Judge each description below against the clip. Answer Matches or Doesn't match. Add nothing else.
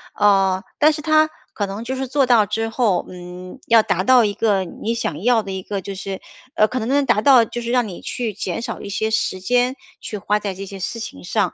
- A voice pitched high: Matches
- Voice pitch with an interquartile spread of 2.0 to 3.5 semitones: Doesn't match